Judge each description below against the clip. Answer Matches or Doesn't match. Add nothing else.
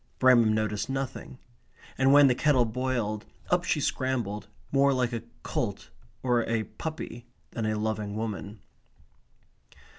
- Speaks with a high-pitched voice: Doesn't match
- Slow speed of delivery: Matches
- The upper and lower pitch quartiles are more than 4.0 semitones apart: Doesn't match